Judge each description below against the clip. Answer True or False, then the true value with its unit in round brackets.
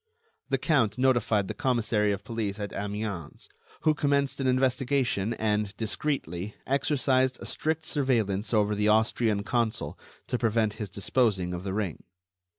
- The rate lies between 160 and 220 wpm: False (145 wpm)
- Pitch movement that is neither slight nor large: True (4.1 semitones)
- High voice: False (110 Hz)